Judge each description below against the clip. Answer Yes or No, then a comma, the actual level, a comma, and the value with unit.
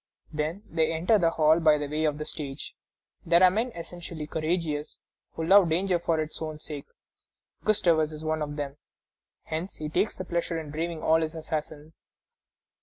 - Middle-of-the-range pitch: Yes, medium, 160 Hz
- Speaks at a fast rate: No, average, 170 wpm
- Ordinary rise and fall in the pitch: No, narrow, 1.9 semitones